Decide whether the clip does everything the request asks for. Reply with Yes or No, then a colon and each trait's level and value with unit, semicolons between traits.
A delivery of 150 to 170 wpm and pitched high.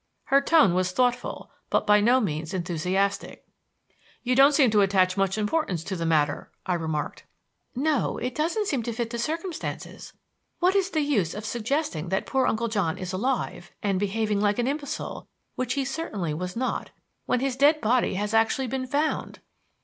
No: average, 180 wpm; high, 225 Hz